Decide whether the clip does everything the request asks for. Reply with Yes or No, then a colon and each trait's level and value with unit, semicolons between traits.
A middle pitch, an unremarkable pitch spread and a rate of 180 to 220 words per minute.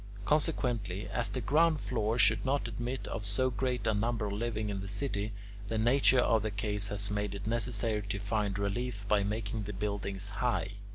No: low, 110 Hz; average, 3.0 semitones; average, 185 wpm